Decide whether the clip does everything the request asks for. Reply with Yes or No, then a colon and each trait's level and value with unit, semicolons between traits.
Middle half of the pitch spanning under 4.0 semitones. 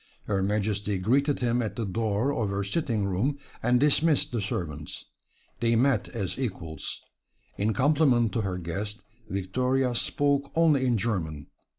No: average, 5.0 semitones